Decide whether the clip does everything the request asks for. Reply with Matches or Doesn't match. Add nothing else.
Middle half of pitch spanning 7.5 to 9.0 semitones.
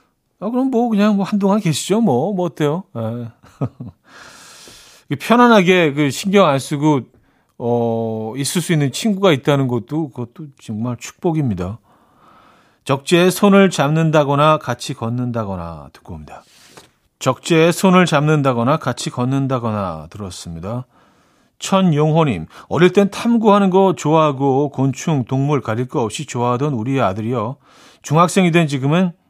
Doesn't match